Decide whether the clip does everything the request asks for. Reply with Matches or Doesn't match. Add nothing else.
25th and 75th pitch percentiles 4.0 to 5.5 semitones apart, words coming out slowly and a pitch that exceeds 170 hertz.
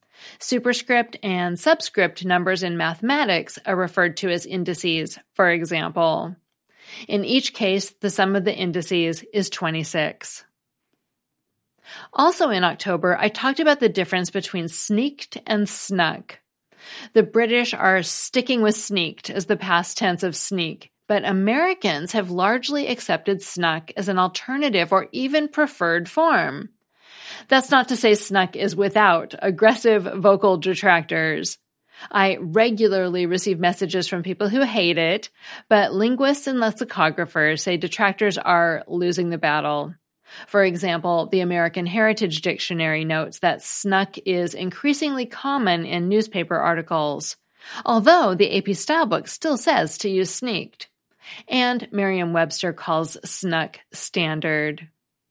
Matches